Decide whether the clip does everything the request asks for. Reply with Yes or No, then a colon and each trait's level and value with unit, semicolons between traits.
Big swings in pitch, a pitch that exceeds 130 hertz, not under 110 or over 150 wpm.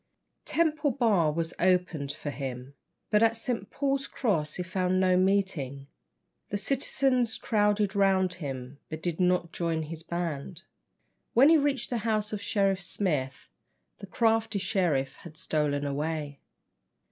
Yes: wide, 5.9 semitones; medium, 185 Hz; average, 140 wpm